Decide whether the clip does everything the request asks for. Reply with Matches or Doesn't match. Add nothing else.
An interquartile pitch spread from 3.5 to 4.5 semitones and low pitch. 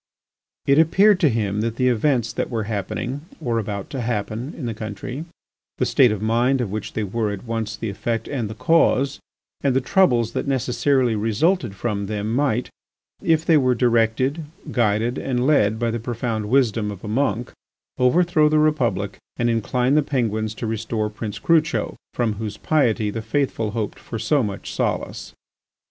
Matches